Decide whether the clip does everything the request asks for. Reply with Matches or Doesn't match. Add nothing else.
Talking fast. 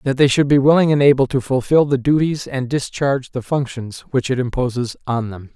Matches